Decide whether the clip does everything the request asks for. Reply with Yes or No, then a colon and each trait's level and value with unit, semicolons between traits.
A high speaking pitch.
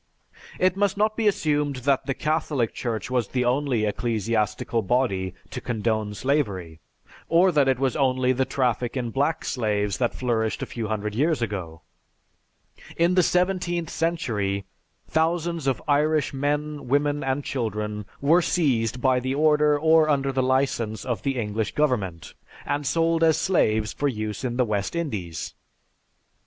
No: low, 130 Hz